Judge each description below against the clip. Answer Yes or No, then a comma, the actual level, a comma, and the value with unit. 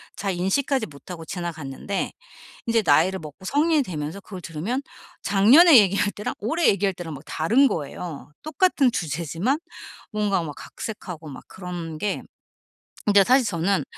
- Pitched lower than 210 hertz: Yes, high, 190 Hz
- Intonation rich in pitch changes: Yes, wide, 5.7 semitones